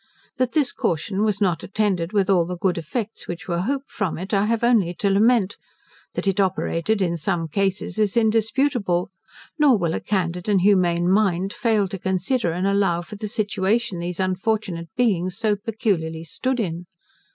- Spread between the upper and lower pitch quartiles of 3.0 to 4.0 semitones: Yes, average, 3.7 semitones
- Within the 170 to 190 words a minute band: Yes, average, 175 wpm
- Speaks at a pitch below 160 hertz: No, high, 195 Hz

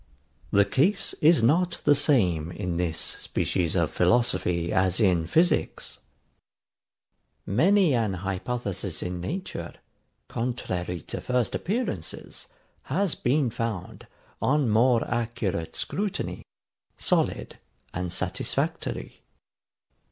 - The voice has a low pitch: Yes, low, 110 Hz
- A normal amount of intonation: No, wide, 7.6 semitones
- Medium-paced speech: No, slow, 100 wpm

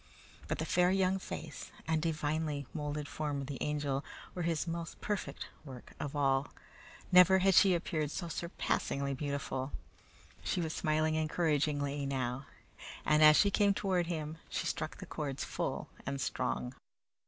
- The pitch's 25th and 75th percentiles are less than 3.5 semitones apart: Yes, average, 3.1 semitones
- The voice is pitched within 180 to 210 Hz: No, medium, 155 Hz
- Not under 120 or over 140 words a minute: No, average, 155 wpm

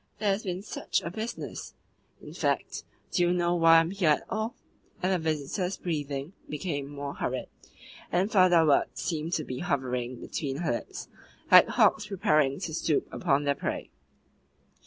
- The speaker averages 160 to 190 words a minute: Yes, average, 170 wpm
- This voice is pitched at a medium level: Yes, medium, 165 Hz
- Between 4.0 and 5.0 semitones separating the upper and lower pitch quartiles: Yes, average, 4.3 semitones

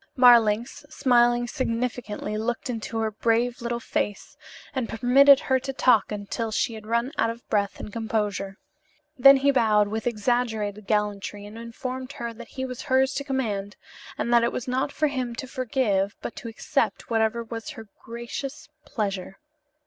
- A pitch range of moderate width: Yes, average, 3.0 semitones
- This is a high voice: Yes, high, 235 Hz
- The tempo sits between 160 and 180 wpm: Yes, average, 170 wpm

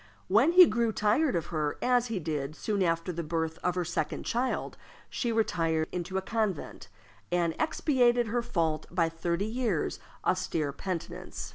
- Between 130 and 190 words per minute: Yes, average, 160 wpm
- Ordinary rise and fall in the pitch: No, wide, 6.0 semitones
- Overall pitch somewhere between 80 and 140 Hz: No, medium, 185 Hz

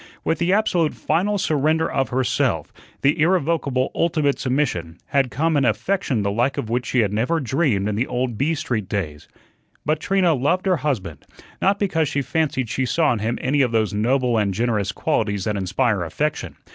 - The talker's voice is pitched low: Yes, low, 130 Hz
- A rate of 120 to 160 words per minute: No, average, 185 wpm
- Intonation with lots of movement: Yes, wide, 6.3 semitones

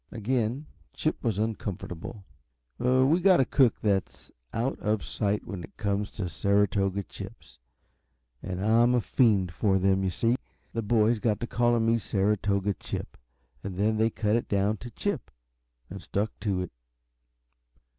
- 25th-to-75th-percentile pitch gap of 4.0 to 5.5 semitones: No, average, 2.9 semitones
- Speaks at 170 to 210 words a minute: No, average, 155 wpm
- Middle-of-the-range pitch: No, low, 105 Hz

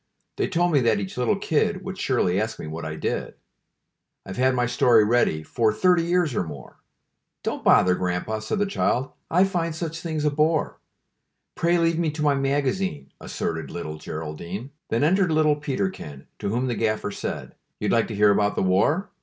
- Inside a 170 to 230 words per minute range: Yes, average, 190 wpm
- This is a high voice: No, low, 130 Hz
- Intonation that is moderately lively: No, wide, 8.4 semitones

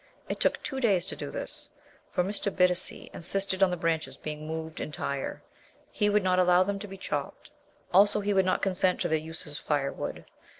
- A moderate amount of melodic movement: Yes, average, 3.5 semitones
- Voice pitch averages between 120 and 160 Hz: No, medium, 180 Hz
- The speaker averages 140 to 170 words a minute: No, average, 200 wpm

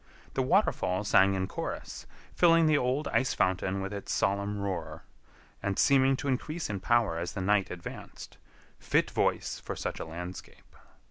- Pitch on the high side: No, low, 100 Hz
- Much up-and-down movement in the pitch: Yes, wide, 6.0 semitones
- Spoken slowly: No, average, 155 wpm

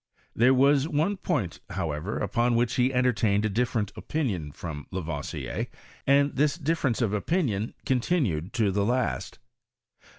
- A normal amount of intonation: No, wide, 6.0 semitones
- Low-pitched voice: Yes, low, 120 Hz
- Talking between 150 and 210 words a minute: No, average, 140 wpm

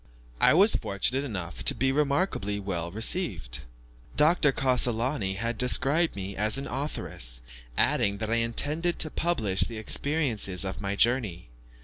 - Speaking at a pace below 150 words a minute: Yes, average, 140 wpm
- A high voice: No, low, 115 Hz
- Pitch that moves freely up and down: Yes, wide, 6.5 semitones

